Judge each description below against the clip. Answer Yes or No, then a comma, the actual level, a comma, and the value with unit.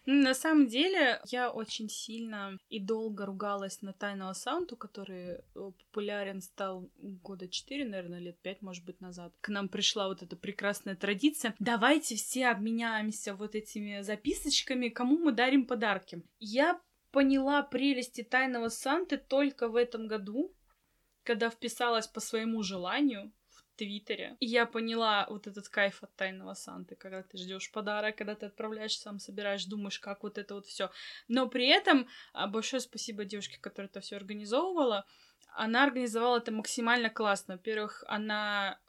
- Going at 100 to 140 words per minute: No, average, 150 wpm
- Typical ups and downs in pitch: Yes, average, 3.6 semitones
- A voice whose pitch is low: No, high, 215 Hz